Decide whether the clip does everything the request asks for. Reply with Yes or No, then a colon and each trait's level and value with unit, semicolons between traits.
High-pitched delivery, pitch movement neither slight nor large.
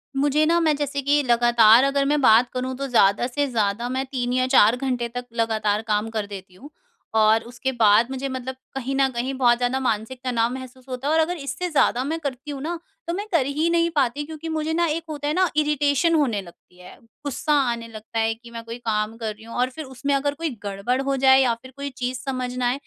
Yes: very high, 255 Hz; average, 3.6 semitones